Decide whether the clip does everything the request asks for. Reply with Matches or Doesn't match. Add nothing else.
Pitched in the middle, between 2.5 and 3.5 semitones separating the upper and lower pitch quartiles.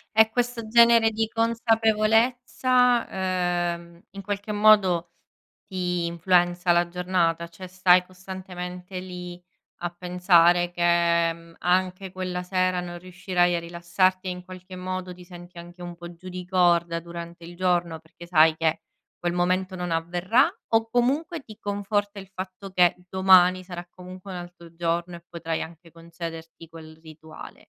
Doesn't match